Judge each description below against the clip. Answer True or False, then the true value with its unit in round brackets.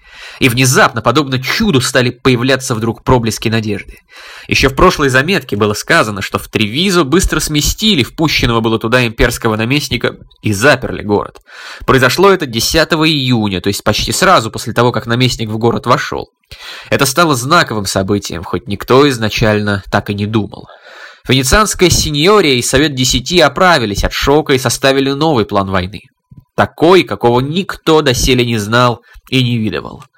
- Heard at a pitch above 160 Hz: False (125 Hz)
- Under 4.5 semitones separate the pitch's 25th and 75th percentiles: False (4.9 semitones)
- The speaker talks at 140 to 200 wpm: True (155 wpm)